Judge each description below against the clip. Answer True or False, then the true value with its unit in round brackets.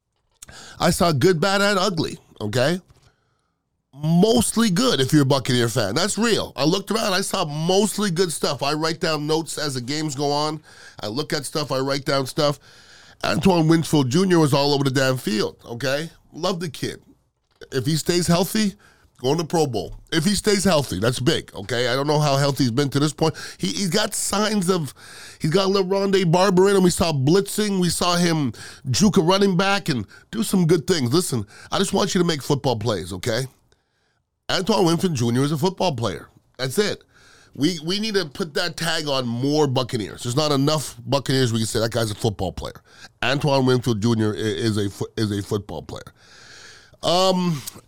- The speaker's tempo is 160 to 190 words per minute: False (200 wpm)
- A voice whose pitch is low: False (155 Hz)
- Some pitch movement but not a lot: False (6.1 semitones)